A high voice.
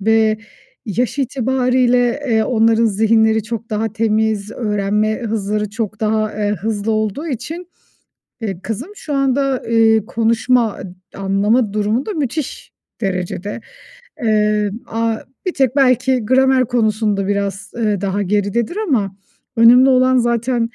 Yes: high, 225 Hz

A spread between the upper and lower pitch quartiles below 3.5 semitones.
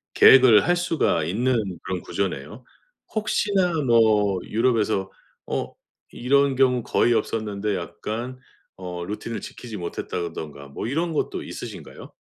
No: average, 5.3 semitones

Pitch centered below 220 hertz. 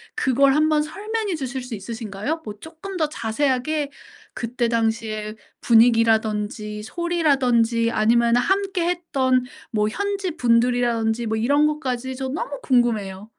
No: high, 245 Hz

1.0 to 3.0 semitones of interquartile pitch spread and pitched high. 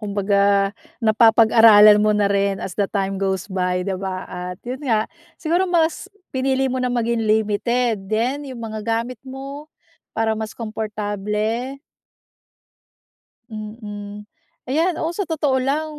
No: average, 4.1 semitones; high, 220 Hz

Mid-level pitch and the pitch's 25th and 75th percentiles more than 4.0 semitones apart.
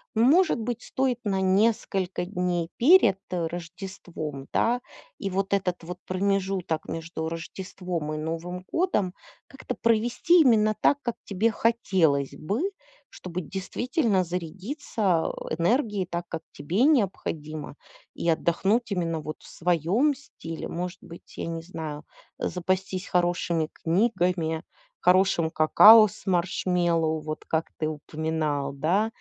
Yes: medium, 180 Hz; average, 4.5 semitones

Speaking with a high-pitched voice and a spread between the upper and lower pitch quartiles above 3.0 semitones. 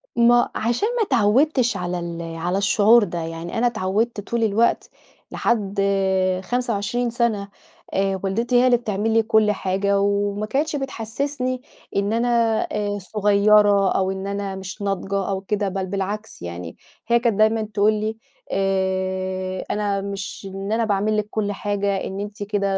No: high, 205 Hz; narrow, 2.6 semitones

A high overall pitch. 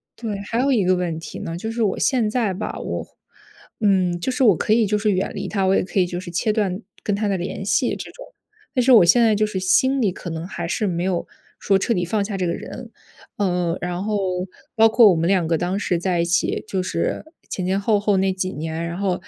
Yes: high, 195 Hz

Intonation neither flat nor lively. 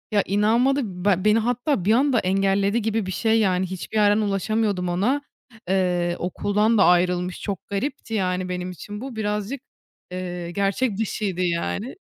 Yes: average, 3.4 semitones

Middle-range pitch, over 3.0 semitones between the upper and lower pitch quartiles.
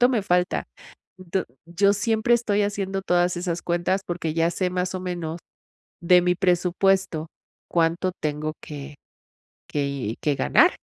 No: medium, 180 Hz; average, 2.7 semitones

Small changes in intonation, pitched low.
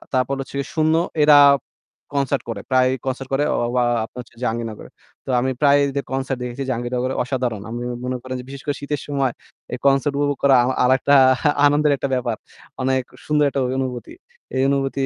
Yes: narrow, 1.9 semitones; low, 130 Hz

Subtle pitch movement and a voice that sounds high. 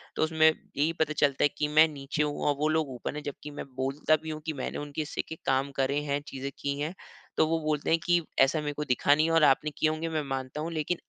No: narrow, 2.0 semitones; medium, 150 Hz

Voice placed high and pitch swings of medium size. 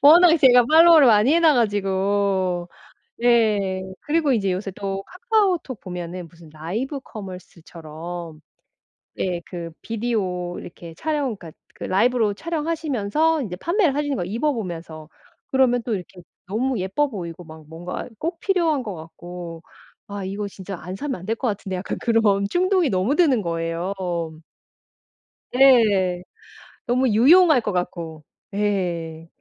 No: high, 205 Hz; wide, 7.1 semitones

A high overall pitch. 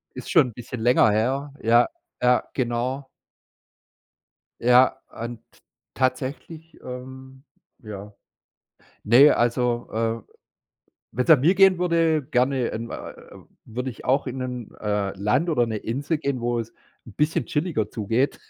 No: low, 125 Hz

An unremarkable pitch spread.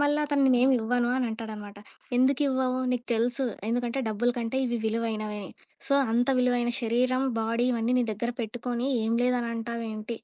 No: narrow, 1.9 semitones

